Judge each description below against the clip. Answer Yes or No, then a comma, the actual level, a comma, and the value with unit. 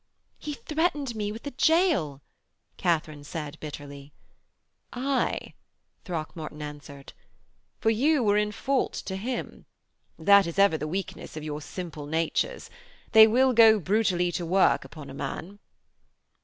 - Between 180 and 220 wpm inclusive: No, slow, 135 wpm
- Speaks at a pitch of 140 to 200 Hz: Yes, high, 190 Hz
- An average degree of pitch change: No, wide, 6.9 semitones